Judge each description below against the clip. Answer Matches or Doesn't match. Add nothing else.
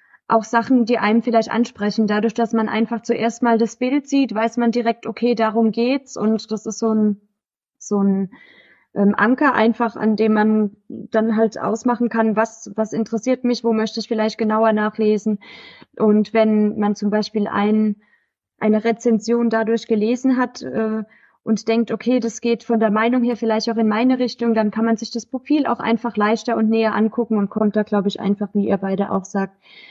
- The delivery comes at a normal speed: Doesn't match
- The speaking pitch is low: Doesn't match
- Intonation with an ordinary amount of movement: Doesn't match